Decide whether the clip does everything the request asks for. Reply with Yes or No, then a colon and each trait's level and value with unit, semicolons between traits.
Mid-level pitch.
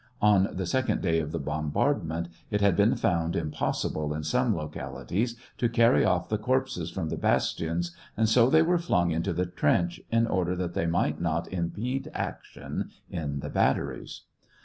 No: very low, 90 Hz